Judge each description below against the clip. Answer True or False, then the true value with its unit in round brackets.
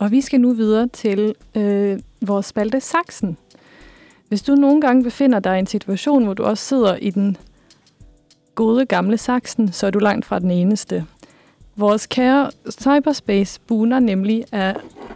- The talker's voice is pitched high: True (220 Hz)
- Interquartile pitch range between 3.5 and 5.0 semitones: True (4.2 semitones)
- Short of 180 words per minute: True (160 wpm)